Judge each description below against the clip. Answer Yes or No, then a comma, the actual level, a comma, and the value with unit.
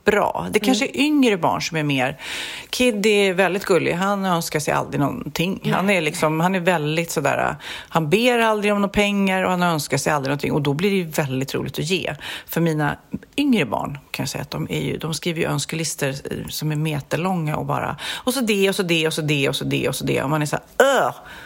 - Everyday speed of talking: No, fast, 250 wpm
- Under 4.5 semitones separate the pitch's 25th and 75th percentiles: No, average, 4.9 semitones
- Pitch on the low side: No, medium, 170 Hz